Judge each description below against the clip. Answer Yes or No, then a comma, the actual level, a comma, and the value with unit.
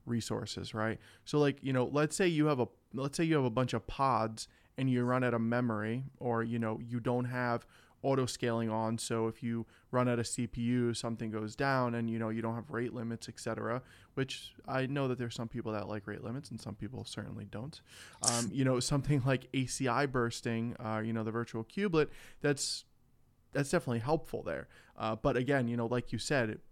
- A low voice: Yes, low, 120 Hz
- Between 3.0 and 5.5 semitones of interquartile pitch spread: No, narrow, 2.5 semitones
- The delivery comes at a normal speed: No, fast, 215 wpm